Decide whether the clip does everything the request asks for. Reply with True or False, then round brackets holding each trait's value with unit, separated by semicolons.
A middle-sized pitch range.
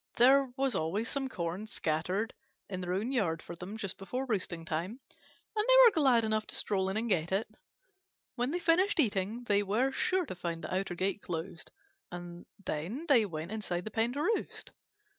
False (6.1 semitones)